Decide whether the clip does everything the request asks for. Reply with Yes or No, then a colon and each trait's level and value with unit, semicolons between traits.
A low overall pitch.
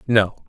Yes: low, 110 Hz